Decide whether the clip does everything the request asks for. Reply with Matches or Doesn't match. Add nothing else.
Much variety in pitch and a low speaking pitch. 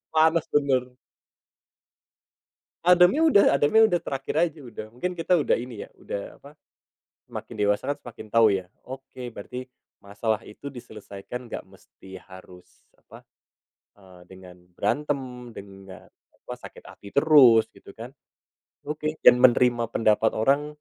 Matches